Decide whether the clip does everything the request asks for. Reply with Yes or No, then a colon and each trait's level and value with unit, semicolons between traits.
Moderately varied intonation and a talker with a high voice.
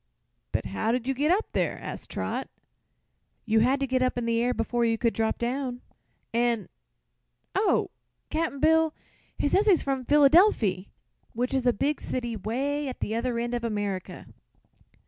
Yes: average, 3.4 semitones; high, 245 Hz